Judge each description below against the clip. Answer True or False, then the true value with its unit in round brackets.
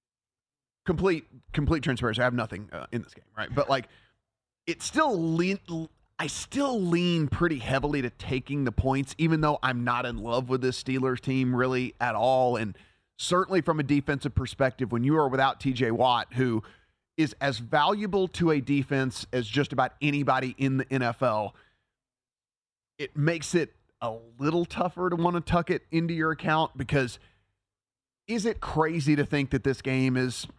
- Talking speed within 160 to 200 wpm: True (175 wpm)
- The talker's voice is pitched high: False (135 Hz)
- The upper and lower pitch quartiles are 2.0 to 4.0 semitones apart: False (4.4 semitones)